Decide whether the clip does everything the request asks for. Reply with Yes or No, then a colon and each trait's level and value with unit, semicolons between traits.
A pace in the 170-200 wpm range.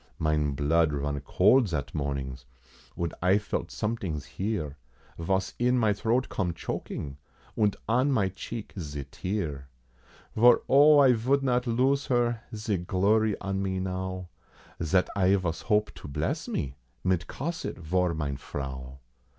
No: average, 145 wpm